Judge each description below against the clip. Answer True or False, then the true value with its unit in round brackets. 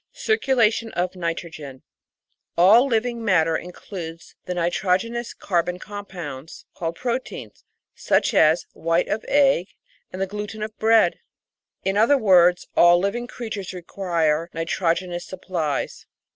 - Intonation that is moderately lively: True (4.5 semitones)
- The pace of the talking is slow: True (115 wpm)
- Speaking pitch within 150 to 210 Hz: True (185 Hz)